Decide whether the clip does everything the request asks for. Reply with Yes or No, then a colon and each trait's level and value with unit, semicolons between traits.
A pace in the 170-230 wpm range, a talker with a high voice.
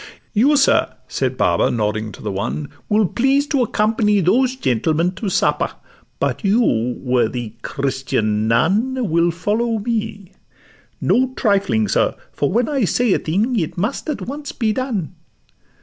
No: average, 150 wpm; high, 205 Hz